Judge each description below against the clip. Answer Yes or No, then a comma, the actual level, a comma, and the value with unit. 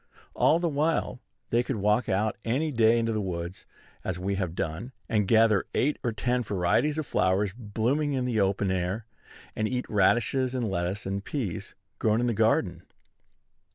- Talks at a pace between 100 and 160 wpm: No, average, 175 wpm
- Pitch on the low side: Yes, low, 110 Hz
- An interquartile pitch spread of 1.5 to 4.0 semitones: No, average, 4.4 semitones